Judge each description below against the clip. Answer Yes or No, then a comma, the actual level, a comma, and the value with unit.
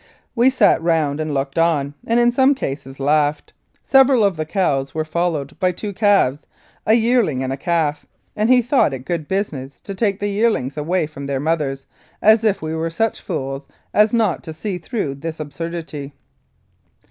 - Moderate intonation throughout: No, wide, 6.5 semitones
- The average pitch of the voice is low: No, medium, 165 Hz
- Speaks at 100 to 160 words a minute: No, average, 180 wpm